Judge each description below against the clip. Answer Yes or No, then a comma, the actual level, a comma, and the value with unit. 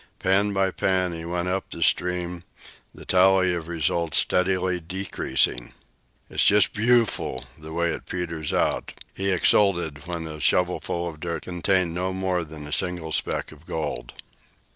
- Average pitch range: No, narrow, 2.3 semitones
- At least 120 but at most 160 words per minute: Yes, average, 155 wpm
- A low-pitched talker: Yes, very low, 90 Hz